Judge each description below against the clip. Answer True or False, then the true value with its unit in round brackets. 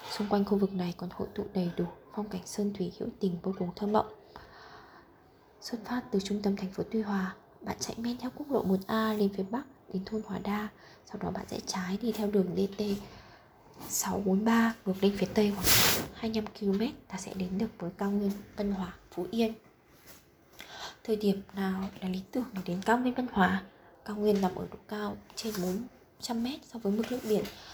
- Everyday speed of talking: True (210 wpm)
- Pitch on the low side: False (205 Hz)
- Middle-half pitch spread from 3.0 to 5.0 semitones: False (2.4 semitones)